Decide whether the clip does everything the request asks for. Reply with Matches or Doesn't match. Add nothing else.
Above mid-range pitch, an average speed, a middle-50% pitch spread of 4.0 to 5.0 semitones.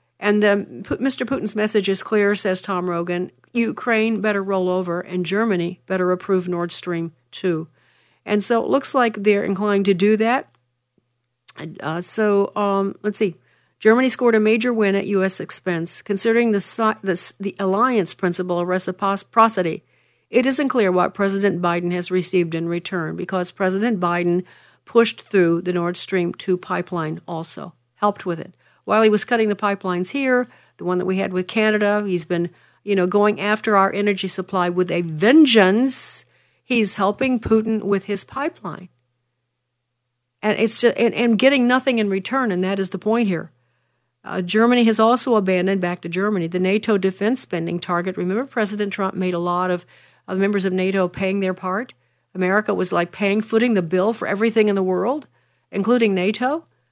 Doesn't match